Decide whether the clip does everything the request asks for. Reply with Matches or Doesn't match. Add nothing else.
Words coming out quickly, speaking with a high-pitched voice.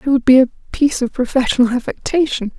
Doesn't match